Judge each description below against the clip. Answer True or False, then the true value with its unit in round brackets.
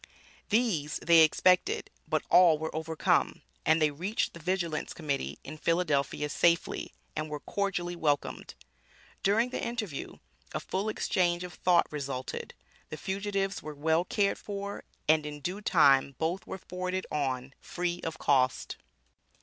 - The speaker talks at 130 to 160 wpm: True (140 wpm)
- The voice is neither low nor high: True (170 Hz)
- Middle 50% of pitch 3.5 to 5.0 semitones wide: True (4.0 semitones)